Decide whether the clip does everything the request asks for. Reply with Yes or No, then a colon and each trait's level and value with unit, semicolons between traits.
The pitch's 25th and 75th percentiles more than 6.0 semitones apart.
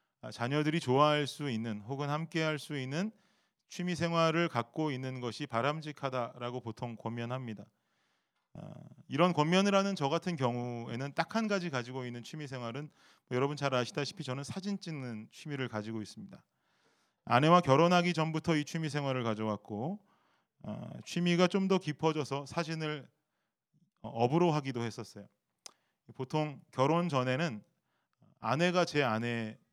No: wide, 5.4 semitones